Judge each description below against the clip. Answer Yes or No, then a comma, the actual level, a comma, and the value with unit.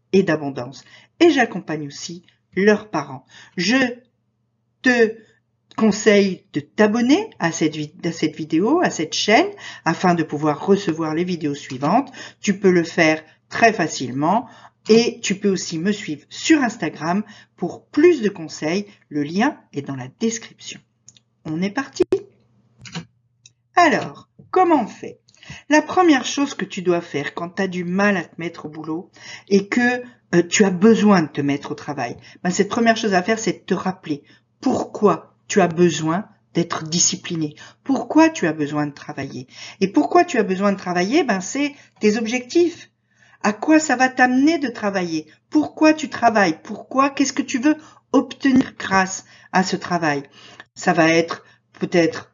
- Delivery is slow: No, average, 165 wpm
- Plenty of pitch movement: Yes, wide, 7.5 semitones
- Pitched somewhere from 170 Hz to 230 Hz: Yes, high, 190 Hz